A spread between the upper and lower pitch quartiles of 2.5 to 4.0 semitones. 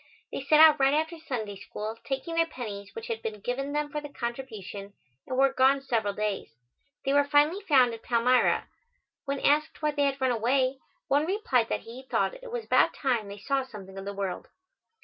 No: average, 4.7 semitones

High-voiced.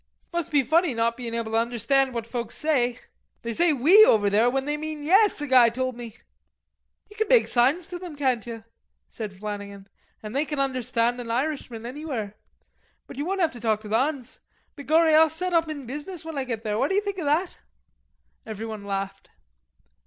Yes: very high, 260 Hz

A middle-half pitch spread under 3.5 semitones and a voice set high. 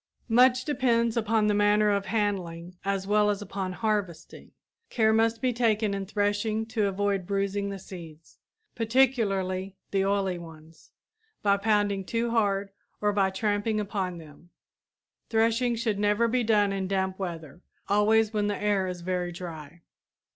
Yes: narrow, 2.6 semitones; high, 205 Hz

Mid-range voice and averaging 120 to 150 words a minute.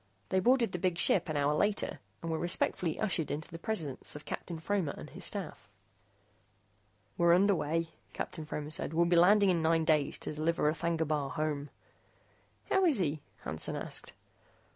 No: medium, 165 Hz; average, 170 wpm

